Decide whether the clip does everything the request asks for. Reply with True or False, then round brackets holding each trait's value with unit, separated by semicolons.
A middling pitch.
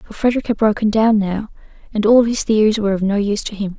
False (215 Hz)